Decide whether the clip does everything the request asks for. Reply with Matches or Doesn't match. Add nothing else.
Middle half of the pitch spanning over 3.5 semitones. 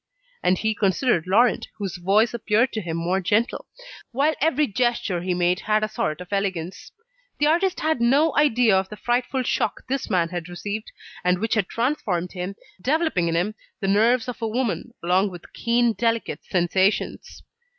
Matches